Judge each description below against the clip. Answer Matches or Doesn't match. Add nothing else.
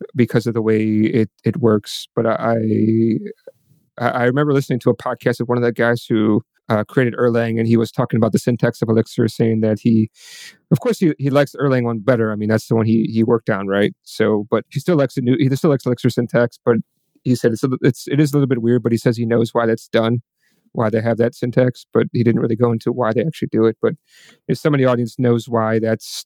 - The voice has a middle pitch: Doesn't match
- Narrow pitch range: Matches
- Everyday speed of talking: Doesn't match